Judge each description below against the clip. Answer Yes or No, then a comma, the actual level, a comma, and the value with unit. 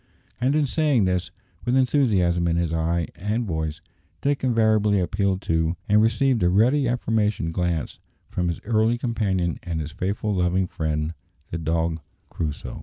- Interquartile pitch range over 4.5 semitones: Yes, average, 5.2 semitones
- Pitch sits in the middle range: No, very low, 95 Hz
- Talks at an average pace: Yes, average, 155 wpm